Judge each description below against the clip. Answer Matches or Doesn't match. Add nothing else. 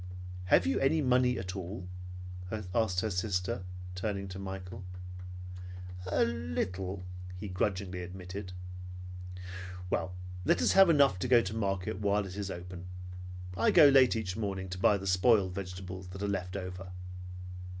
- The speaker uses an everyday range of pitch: Doesn't match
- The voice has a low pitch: Matches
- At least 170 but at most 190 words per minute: Doesn't match